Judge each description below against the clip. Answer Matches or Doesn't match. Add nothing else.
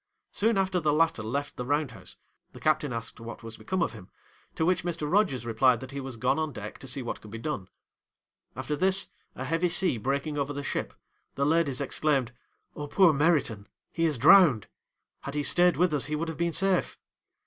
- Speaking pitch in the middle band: Matches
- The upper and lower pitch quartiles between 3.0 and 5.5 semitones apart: Matches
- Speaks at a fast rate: Matches